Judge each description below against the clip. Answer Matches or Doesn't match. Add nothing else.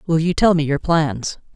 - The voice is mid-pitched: Matches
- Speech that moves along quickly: Matches